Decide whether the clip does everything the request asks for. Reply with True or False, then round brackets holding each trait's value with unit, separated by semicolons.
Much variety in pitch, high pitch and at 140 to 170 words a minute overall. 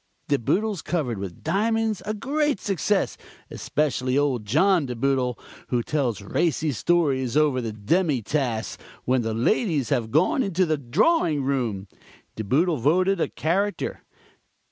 False (7.1 semitones; 145 Hz; 145 wpm)